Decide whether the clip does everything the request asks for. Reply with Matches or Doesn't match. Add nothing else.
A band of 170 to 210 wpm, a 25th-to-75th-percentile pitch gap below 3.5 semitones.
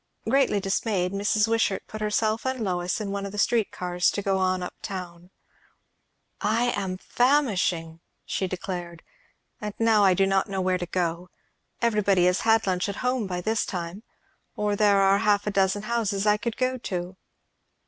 Matches